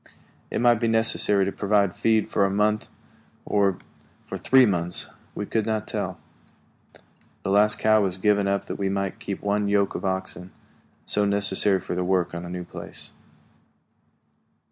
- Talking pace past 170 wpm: No, average, 165 wpm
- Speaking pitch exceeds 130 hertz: No, low, 100 Hz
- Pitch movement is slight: Yes, narrow, 1.7 semitones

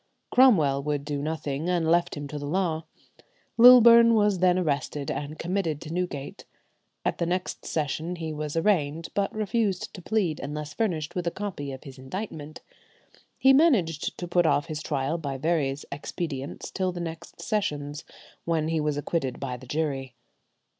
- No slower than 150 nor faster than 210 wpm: Yes, average, 165 wpm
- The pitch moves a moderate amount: Yes, average, 3.9 semitones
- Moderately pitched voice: Yes, medium, 160 Hz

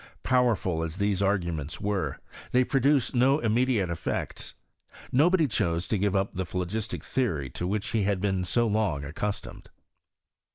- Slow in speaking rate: No, average, 150 wpm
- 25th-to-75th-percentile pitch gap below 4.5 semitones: No, average, 5.0 semitones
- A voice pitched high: No, low, 100 Hz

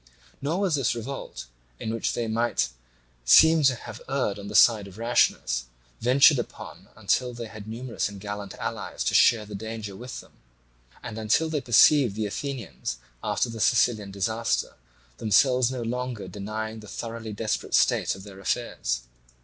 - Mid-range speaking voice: No, low, 115 Hz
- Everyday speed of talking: Yes, average, 165 wpm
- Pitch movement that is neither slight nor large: Yes, average, 3.4 semitones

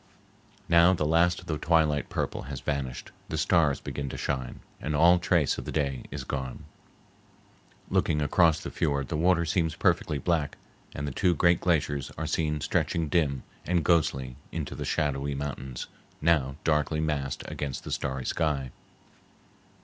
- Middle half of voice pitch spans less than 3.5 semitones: Yes, average, 3.0 semitones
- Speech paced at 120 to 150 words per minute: No, average, 160 wpm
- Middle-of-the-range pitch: No, very low, 75 Hz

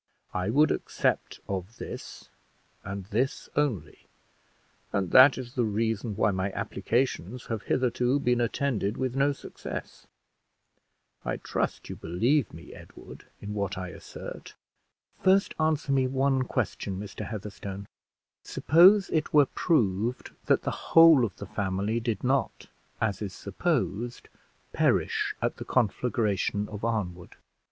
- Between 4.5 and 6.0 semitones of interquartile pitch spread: Yes, average, 5.0 semitones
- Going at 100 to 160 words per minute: Yes, slow, 135 wpm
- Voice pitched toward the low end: Yes, low, 115 Hz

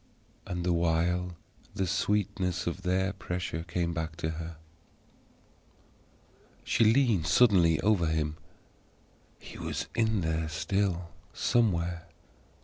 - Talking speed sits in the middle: No, slow, 110 wpm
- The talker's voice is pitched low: Yes, very low, 90 Hz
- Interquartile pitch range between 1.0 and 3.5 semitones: Yes, average, 2.8 semitones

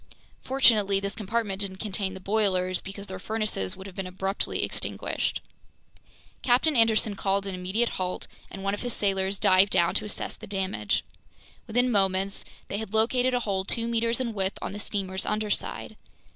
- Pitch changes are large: No, narrow, 2.5 semitones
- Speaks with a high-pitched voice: Yes, high, 200 Hz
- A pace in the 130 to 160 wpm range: No, average, 170 wpm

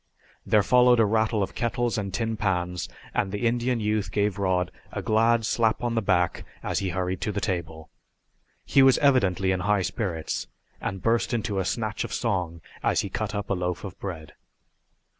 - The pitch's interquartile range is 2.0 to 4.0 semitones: Yes, average, 3.6 semitones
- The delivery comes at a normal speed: Yes, average, 190 wpm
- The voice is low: Yes, low, 100 Hz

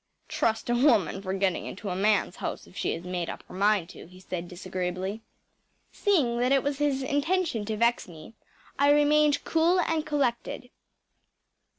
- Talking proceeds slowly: No, average, 175 wpm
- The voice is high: Yes, high, 230 Hz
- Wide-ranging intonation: Yes, wide, 7.5 semitones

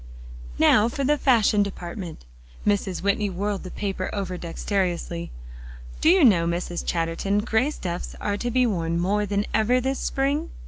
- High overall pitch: Yes, high, 200 Hz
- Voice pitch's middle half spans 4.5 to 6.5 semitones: Yes, average, 4.9 semitones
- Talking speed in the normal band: Yes, average, 155 wpm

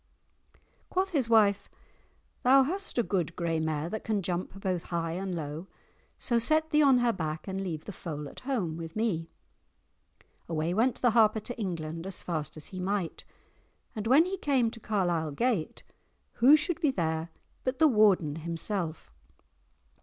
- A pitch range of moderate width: No, wide, 6.7 semitones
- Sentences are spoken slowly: No, average, 175 wpm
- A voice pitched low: No, high, 195 Hz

